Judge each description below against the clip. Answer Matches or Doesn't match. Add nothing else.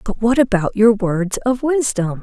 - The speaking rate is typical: Matches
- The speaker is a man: Doesn't match